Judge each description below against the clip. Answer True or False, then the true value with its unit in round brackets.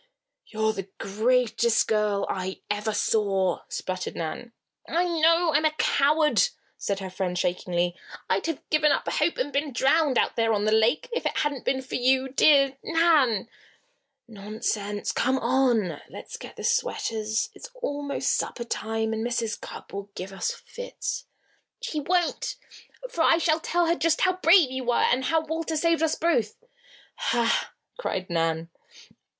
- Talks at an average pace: True (160 wpm)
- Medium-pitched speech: False (255 Hz)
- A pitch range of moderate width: False (7.0 semitones)